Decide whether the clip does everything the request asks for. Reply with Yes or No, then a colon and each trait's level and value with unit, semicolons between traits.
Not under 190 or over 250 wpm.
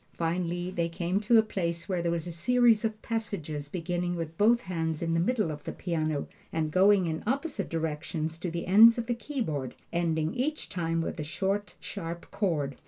Yes: average, 195 wpm